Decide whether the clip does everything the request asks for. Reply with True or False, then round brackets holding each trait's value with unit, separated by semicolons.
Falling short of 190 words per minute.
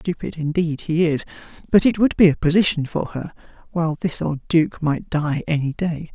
False (195 wpm)